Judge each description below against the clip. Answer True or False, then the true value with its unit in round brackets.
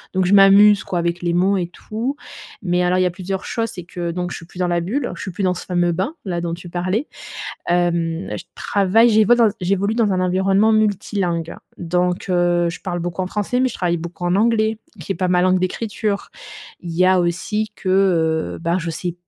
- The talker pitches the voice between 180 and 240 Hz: True (185 Hz)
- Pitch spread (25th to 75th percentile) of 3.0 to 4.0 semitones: False (2.5 semitones)